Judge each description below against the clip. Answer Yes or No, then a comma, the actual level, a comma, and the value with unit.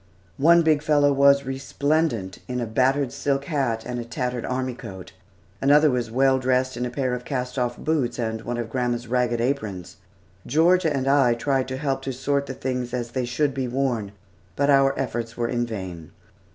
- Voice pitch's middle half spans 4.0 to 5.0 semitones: No, narrow, 2.6 semitones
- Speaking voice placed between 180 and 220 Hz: No, low, 130 Hz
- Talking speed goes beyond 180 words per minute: Yes, average, 190 wpm